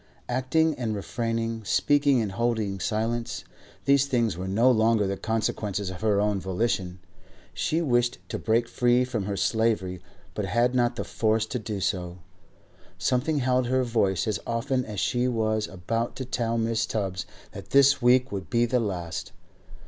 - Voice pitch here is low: Yes, low, 115 Hz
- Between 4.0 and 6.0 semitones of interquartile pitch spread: No, average, 3.2 semitones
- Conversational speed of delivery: Yes, average, 165 wpm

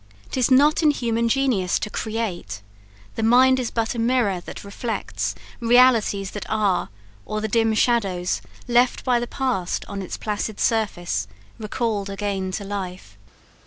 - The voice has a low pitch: No, high, 220 Hz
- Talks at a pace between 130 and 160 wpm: Yes, average, 150 wpm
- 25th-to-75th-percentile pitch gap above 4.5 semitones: No, average, 3.5 semitones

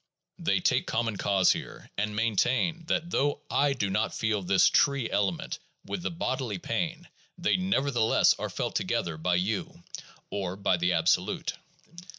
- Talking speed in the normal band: Yes, average, 155 wpm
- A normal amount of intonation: No, wide, 6.7 semitones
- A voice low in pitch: Yes, low, 110 Hz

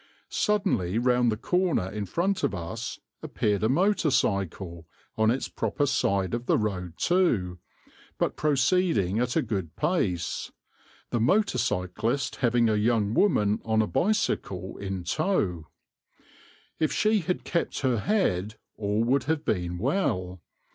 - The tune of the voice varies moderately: No, wide, 8.1 semitones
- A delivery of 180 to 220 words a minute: No, average, 140 wpm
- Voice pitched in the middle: No, low, 115 Hz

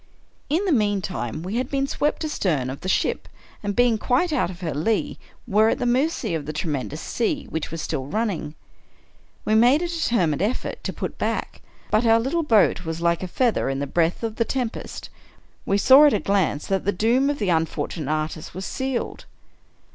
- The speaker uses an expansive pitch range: Yes, wide, 7.5 semitones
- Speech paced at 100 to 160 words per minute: No, average, 200 wpm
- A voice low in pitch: No, high, 205 Hz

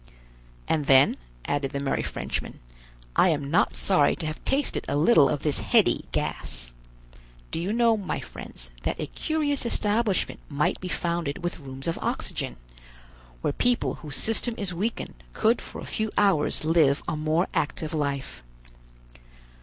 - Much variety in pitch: Yes, wide, 6.6 semitones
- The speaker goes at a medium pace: Yes, average, 155 wpm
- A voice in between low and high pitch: Yes, medium, 165 Hz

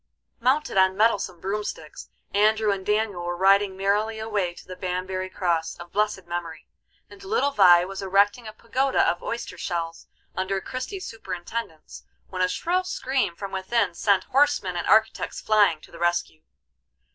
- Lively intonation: No, average, 3.5 semitones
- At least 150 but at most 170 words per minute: Yes, average, 155 wpm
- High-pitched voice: Yes, high, 195 Hz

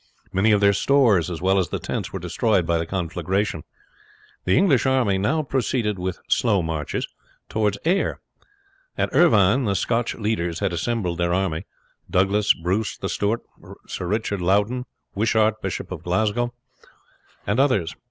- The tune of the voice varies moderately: Yes, average, 3.9 semitones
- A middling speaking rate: Yes, average, 150 wpm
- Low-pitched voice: Yes, low, 100 Hz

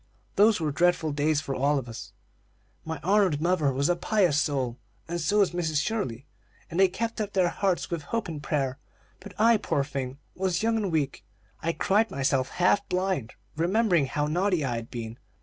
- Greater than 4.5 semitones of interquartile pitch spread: Yes, wide, 5.4 semitones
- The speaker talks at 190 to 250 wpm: Yes, average, 195 wpm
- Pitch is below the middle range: No, medium, 160 Hz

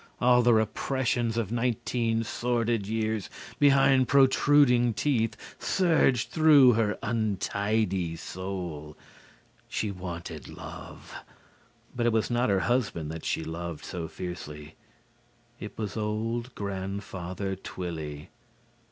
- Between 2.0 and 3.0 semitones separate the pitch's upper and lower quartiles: No, average, 4.7 semitones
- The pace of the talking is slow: Yes, slow, 110 wpm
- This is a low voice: Yes, low, 110 Hz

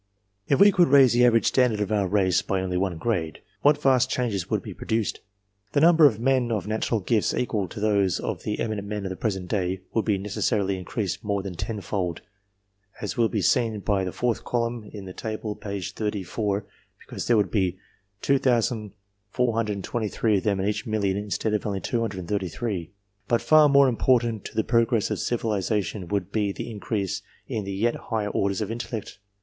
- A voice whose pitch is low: Yes, low, 105 Hz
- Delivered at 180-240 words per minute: Yes, average, 185 wpm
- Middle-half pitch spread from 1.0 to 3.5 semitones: Yes, average, 3.0 semitones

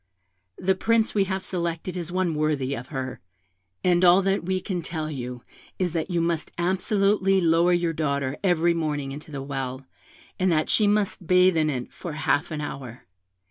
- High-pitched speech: No, medium, 170 Hz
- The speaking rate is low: No, average, 180 wpm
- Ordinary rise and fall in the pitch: Yes, average, 4.0 semitones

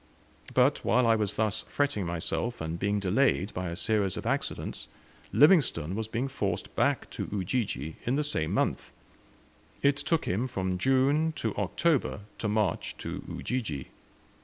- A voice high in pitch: No, low, 110 Hz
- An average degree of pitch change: No, wide, 6.2 semitones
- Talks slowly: No, average, 155 wpm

